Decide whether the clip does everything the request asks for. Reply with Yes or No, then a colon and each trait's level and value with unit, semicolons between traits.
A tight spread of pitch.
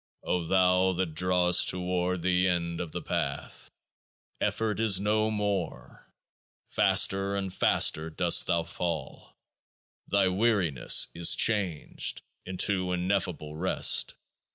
Yes: narrow, 2.2 semitones